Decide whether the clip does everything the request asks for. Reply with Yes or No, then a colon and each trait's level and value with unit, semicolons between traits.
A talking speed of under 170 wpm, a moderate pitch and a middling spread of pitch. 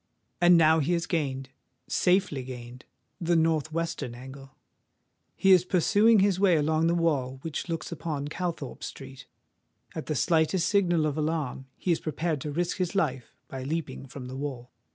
Yes: average, 160 wpm; medium, 160 Hz; average, 4.3 semitones